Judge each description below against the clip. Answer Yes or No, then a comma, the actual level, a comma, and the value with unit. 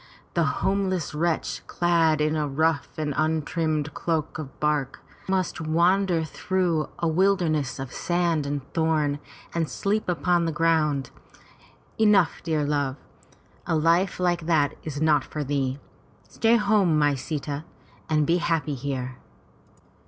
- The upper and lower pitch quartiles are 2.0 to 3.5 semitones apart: Yes, average, 2.8 semitones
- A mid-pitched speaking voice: Yes, medium, 160 Hz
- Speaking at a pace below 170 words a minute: Yes, slow, 135 wpm